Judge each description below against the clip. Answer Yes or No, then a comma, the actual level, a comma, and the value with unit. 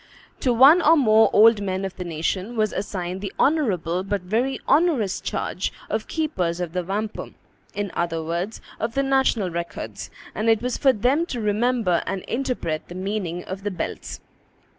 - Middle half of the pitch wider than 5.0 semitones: Yes, wide, 5.4 semitones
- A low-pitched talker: No, high, 205 Hz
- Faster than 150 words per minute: Yes, average, 175 wpm